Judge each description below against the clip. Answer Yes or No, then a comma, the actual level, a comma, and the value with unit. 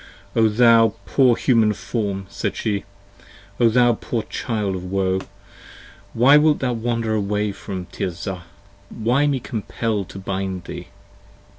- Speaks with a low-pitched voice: Yes, low, 110 Hz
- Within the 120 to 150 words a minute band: Yes, average, 140 wpm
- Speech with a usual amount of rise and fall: Yes, average, 3.6 semitones